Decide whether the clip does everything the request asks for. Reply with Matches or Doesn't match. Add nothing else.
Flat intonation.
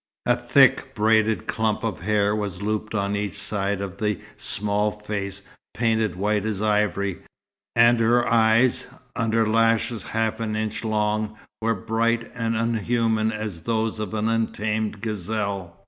Matches